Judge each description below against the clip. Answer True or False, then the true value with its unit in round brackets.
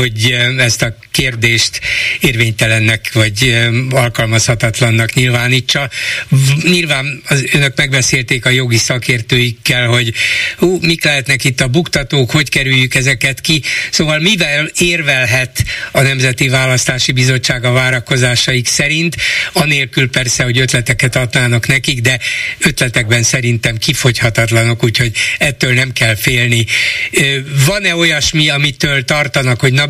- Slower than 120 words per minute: True (110 wpm)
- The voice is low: True (130 Hz)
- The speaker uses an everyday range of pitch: True (3.1 semitones)